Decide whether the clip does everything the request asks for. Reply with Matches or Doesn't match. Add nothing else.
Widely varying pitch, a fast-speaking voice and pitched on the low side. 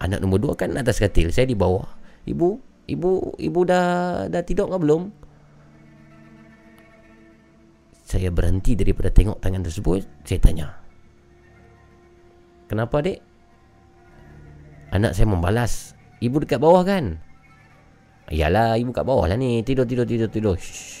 Doesn't match